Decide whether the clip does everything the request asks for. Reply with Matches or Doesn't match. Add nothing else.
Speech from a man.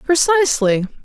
Doesn't match